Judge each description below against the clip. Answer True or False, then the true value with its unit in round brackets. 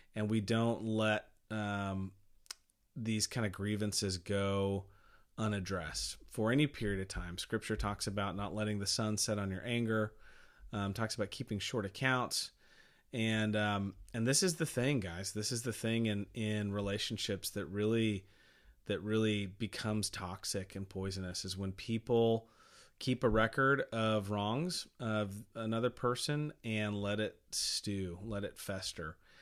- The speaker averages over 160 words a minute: False (150 wpm)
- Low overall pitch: True (105 Hz)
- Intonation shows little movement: True (2.3 semitones)